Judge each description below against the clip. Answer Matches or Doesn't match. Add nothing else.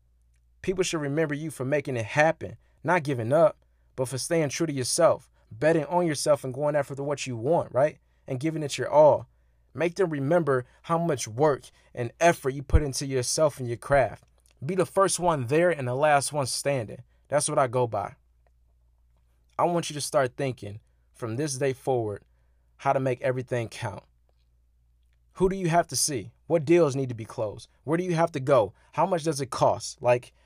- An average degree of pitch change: Doesn't match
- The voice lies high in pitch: Doesn't match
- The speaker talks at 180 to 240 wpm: Matches